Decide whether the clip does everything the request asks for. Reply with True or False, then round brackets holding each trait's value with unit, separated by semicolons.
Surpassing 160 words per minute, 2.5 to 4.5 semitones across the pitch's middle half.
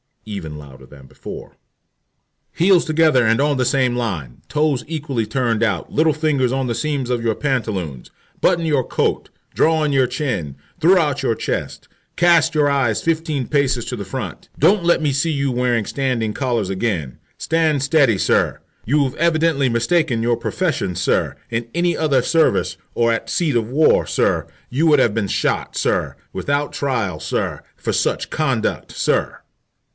False (170 wpm; 5.2 semitones)